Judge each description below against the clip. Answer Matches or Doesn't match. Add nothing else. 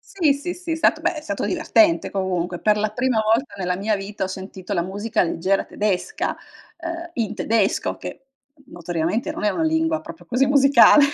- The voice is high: Matches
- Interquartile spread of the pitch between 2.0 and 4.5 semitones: Doesn't match